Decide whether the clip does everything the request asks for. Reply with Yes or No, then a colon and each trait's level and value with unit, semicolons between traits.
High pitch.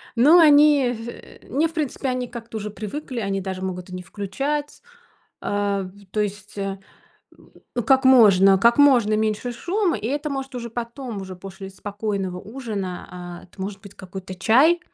Yes: high, 215 Hz